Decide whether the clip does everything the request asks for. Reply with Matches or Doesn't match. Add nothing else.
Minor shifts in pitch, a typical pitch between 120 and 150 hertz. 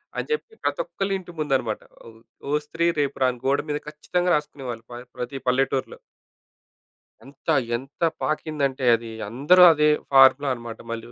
Doesn't match